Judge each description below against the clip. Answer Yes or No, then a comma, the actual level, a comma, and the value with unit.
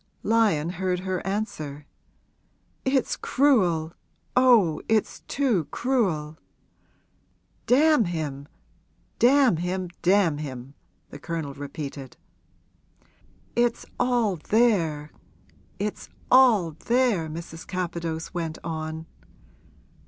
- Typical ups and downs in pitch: No, wide, 6.4 semitones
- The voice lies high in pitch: No, medium, 175 Hz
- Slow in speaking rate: Yes, slow, 85 wpm